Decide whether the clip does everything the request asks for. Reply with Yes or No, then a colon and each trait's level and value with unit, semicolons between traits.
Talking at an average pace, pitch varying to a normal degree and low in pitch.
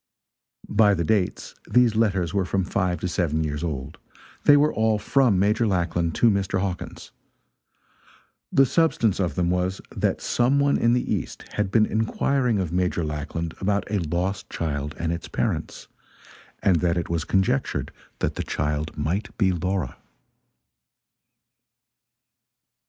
Yes: average, 145 wpm; average, 4.2 semitones; very low, 95 Hz